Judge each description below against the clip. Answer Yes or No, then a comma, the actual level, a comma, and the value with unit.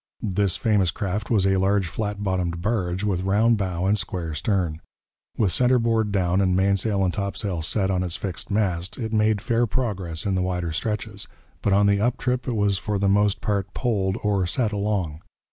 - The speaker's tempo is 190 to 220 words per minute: Yes, average, 195 wpm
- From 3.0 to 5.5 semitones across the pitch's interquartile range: No, narrow, 2.5 semitones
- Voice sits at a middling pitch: No, low, 100 Hz